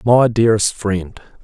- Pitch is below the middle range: Yes, low, 110 Hz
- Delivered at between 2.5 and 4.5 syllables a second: Yes, 4.4 syllables/s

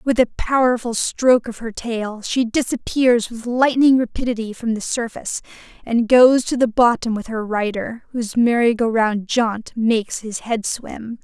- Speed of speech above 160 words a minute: Yes, average, 170 wpm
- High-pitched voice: Yes, high, 230 Hz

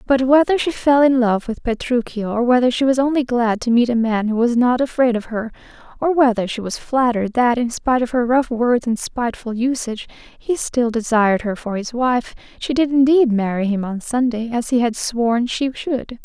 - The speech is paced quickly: Yes, fast, 215 wpm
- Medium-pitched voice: No, high, 240 Hz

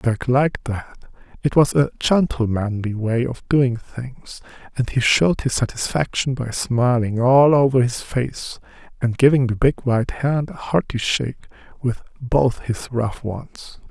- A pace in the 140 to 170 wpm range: Yes, average, 155 wpm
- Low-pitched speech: Yes, low, 125 Hz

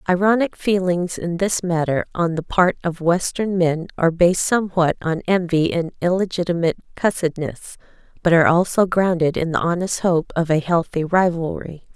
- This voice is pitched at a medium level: Yes, medium, 175 Hz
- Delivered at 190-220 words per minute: No, average, 155 wpm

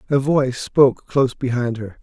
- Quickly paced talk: No, average, 180 wpm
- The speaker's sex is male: Yes, male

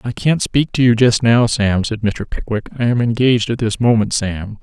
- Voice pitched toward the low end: Yes, low, 115 Hz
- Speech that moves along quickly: Yes, fast, 235 wpm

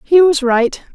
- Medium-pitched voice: No, very high, 290 Hz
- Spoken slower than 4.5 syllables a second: Yes, 4.0 syllables/s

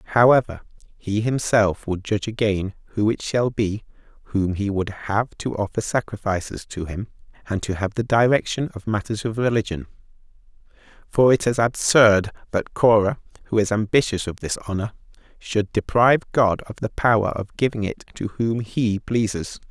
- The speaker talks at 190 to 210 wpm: No, average, 160 wpm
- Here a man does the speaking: Yes, male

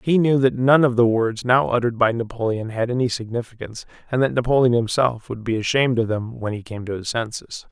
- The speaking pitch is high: No, low, 120 Hz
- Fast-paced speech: Yes, fast, 225 wpm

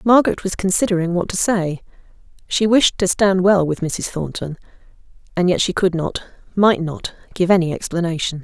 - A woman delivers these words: Yes, female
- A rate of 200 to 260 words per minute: No, average, 170 wpm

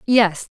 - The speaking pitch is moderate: No, high, 210 Hz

